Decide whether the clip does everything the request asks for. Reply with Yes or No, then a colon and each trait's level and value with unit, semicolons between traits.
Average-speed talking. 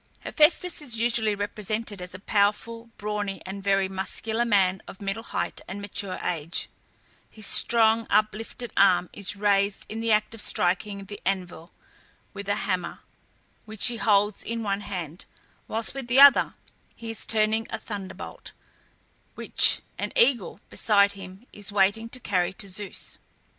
Yes: average, 155 wpm